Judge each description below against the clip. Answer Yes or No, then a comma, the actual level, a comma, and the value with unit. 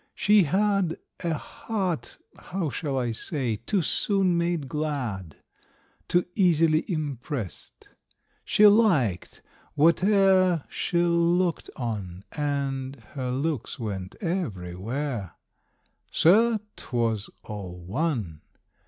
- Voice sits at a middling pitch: Yes, medium, 150 Hz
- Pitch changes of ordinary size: No, wide, 7.3 semitones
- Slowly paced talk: Yes, slow, 95 wpm